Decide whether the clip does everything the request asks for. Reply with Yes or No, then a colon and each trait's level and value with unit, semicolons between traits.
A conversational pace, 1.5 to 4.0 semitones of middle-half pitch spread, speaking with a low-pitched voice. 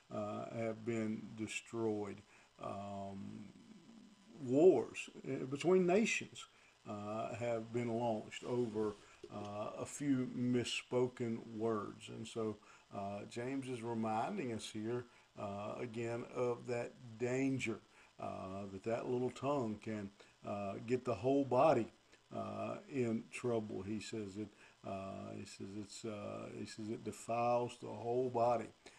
No: slow, 125 wpm; average, 2.8 semitones; low, 115 Hz